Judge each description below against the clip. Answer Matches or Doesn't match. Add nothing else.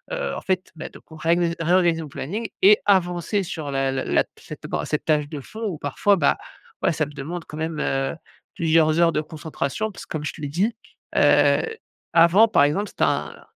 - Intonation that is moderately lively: Matches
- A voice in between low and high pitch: Matches